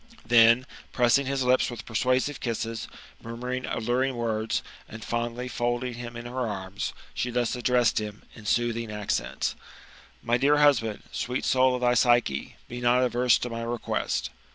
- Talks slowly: No, average, 165 wpm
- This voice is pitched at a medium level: No, low, 120 Hz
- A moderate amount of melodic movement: No, narrow, 1.5 semitones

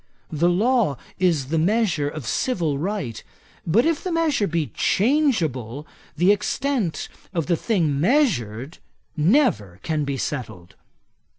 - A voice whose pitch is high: No, medium, 170 Hz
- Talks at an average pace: No, slow, 125 wpm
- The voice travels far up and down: Yes, wide, 8.1 semitones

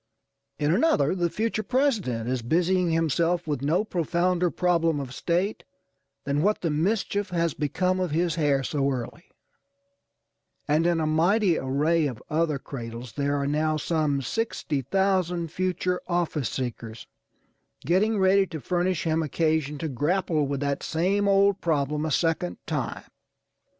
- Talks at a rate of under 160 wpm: Yes, average, 145 wpm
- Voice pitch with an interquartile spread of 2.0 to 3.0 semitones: No, average, 4.0 semitones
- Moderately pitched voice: Yes, medium, 165 Hz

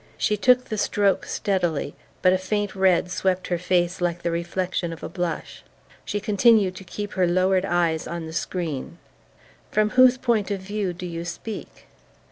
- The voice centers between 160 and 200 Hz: Yes, medium, 185 Hz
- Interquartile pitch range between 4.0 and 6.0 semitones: No, average, 2.9 semitones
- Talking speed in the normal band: Yes, average, 175 wpm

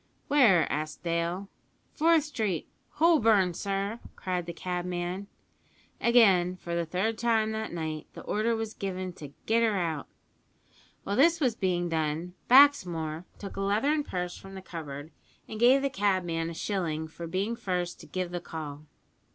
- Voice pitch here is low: No, medium, 185 Hz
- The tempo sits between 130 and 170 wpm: Yes, average, 160 wpm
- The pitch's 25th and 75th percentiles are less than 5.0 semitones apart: Yes, average, 4.6 semitones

